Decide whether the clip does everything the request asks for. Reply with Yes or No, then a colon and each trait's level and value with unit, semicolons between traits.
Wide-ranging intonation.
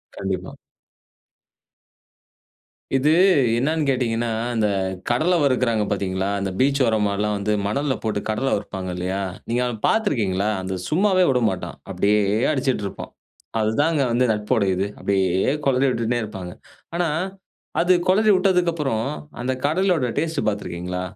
Yes: wide, 6.0 semitones